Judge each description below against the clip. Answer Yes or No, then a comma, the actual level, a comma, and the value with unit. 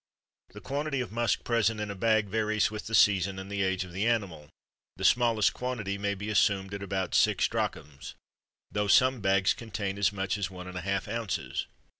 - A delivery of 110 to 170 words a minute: No, average, 200 wpm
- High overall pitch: No, low, 100 Hz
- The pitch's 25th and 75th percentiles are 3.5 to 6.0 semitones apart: No, average, 2.7 semitones